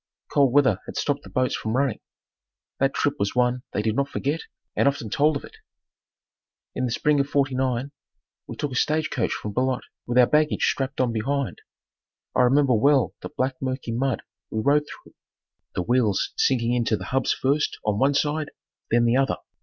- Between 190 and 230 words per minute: Yes, average, 195 wpm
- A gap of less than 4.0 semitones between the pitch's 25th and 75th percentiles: Yes, average, 2.9 semitones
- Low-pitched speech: Yes, low, 130 Hz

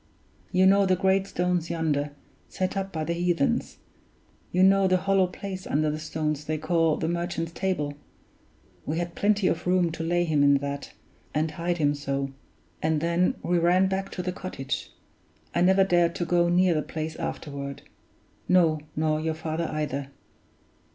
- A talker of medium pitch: Yes, medium, 170 Hz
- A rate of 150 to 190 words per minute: Yes, average, 170 wpm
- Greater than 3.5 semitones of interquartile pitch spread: No, average, 3.0 semitones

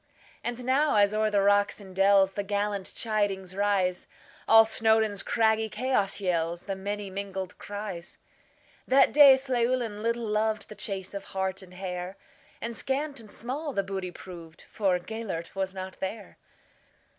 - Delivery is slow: Yes, slow, 130 wpm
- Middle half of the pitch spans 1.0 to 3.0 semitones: Yes, average, 2.7 semitones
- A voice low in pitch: No, high, 205 Hz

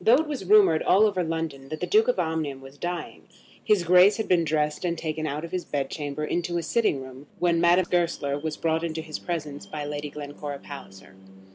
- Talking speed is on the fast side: Yes, fast, 220 wpm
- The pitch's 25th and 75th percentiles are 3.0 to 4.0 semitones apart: Yes, average, 3.3 semitones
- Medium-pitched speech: Yes, medium, 160 Hz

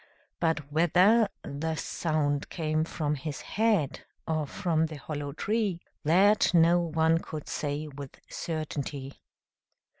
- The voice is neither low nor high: Yes, medium, 160 Hz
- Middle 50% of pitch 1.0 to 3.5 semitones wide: Yes, average, 2.9 semitones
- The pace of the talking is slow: Yes, slow, 120 wpm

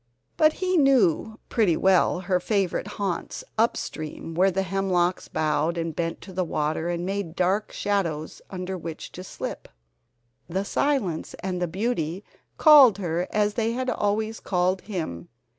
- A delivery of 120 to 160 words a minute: Yes, average, 155 wpm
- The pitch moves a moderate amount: Yes, average, 3.5 semitones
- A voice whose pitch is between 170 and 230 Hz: Yes, medium, 185 Hz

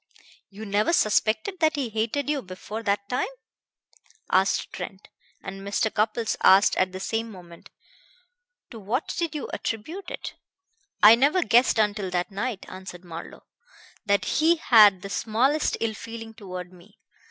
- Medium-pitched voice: No, high, 215 Hz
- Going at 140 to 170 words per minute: Yes, average, 150 wpm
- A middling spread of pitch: Yes, average, 4.0 semitones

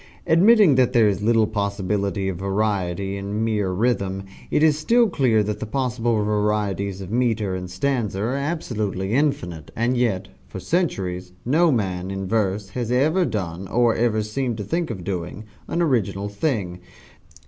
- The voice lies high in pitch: No, low, 105 Hz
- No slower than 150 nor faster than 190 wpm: Yes, average, 160 wpm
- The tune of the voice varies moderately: Yes, average, 4.5 semitones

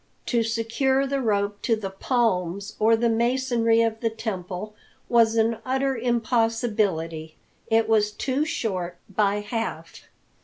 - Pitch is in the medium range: No, high, 225 Hz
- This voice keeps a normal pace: No, slow, 130 wpm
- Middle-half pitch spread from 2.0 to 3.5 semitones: Yes, narrow, 2.6 semitones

